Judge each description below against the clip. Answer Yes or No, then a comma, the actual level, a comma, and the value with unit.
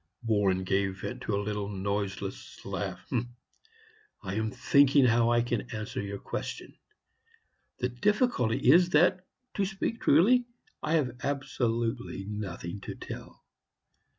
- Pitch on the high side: No, low, 115 Hz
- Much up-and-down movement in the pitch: Yes, wide, 6.0 semitones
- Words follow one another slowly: Yes, slow, 125 wpm